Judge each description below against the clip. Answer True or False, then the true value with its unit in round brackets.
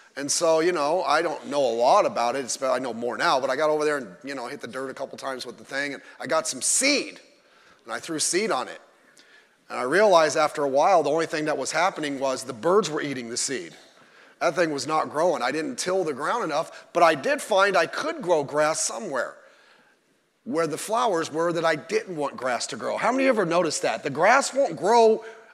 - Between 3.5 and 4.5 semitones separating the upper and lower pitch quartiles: True (4.2 semitones)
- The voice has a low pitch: False (155 Hz)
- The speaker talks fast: True (245 wpm)